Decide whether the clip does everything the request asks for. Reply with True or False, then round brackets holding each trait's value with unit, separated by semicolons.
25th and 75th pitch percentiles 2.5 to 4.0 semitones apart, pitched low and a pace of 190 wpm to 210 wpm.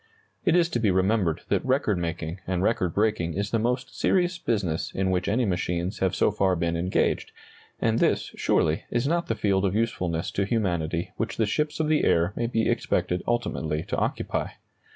False (4.9 semitones; 100 Hz; 195 wpm)